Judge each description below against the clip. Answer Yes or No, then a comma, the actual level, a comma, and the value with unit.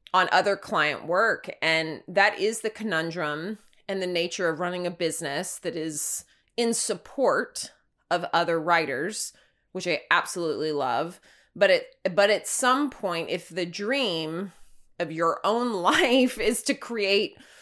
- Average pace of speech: Yes, average, 145 wpm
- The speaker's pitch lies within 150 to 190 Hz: Yes, medium, 185 Hz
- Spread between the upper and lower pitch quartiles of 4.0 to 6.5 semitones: Yes, average, 4.6 semitones